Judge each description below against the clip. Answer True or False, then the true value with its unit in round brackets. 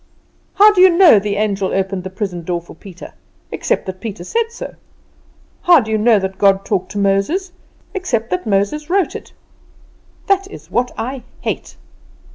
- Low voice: False (210 Hz)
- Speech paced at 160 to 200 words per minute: True (175 wpm)